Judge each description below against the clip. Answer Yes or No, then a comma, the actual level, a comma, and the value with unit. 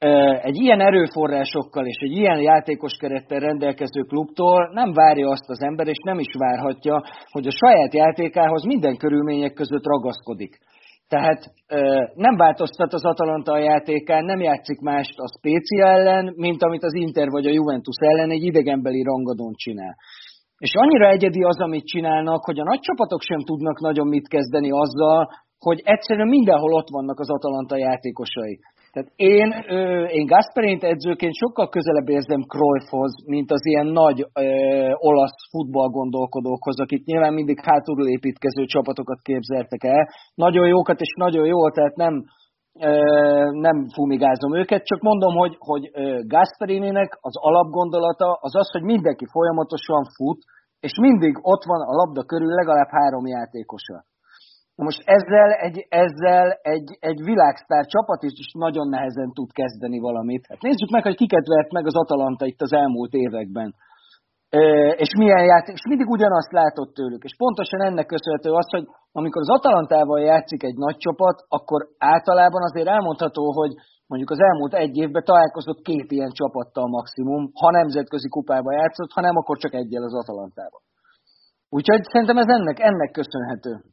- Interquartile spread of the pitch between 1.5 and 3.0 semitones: No, average, 4.0 semitones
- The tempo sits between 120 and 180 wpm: Yes, fast, 155 wpm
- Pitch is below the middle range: No, medium, 155 Hz